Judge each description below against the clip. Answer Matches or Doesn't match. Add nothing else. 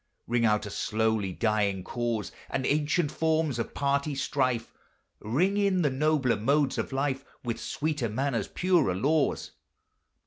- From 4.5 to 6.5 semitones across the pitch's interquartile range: Matches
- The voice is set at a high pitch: Doesn't match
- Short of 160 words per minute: Matches